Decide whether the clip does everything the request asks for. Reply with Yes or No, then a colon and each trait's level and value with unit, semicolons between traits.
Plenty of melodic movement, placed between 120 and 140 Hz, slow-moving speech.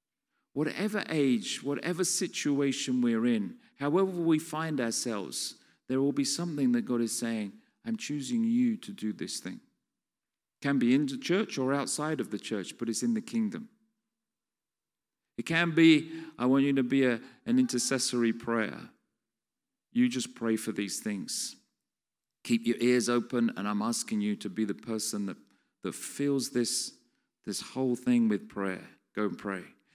No: wide, 8.7 semitones; low, 135 Hz; average, 165 wpm